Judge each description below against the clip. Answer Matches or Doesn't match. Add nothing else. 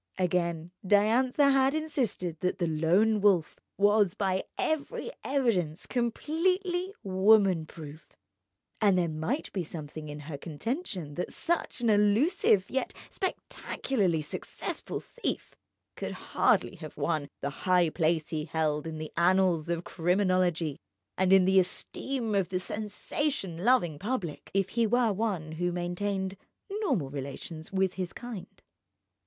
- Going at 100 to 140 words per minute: Matches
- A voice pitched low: Doesn't match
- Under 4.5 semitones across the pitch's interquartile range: Doesn't match